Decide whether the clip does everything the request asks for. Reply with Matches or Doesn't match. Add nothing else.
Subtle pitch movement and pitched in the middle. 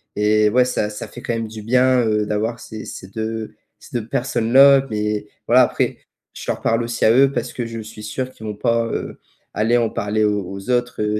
Doesn't match